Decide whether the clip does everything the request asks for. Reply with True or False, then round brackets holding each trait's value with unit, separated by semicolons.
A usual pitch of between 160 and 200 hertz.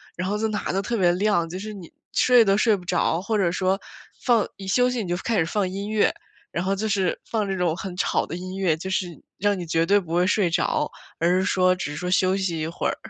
True (190 Hz)